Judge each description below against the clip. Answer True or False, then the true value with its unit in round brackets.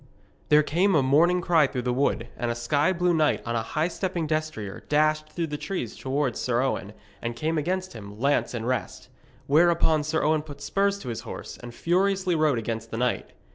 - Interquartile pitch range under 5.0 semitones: False (5.6 semitones)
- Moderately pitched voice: True (150 Hz)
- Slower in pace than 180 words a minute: False (205 wpm)